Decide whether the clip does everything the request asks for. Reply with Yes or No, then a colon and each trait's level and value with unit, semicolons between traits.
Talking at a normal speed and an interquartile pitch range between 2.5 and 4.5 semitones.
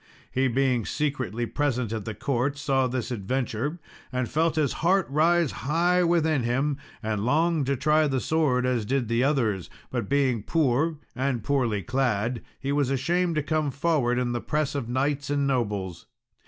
Yes: average, 170 wpm; average, 3.8 semitones